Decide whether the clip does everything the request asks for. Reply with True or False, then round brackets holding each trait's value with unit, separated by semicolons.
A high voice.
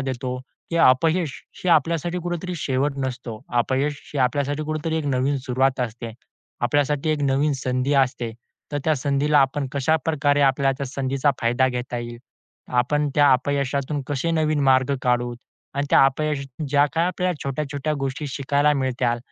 False (140 Hz)